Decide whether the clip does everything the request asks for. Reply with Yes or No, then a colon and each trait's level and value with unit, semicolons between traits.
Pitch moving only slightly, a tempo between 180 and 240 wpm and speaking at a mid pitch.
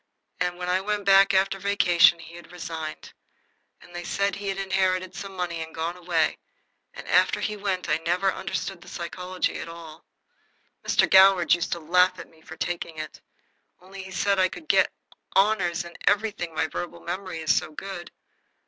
Yes: narrow, 2.3 semitones; average, 185 wpm; medium, 180 Hz